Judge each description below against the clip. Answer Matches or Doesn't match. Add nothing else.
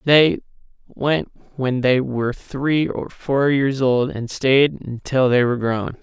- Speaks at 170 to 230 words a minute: Doesn't match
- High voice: Doesn't match